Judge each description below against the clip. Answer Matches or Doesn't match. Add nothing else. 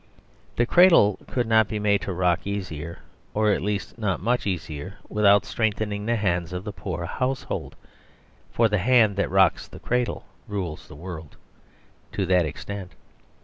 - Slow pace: Doesn't match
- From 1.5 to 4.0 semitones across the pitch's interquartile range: Matches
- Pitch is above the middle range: Doesn't match